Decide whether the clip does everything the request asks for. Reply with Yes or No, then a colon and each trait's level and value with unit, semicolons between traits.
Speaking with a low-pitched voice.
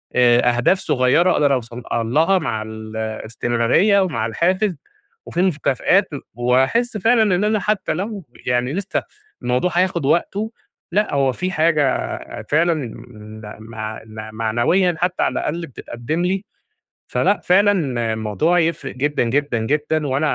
No: medium, 150 Hz